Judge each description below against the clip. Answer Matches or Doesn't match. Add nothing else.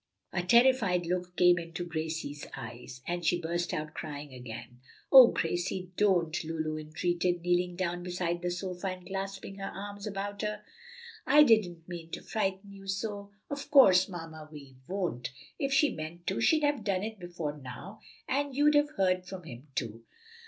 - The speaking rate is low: Doesn't match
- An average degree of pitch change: Matches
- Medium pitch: Matches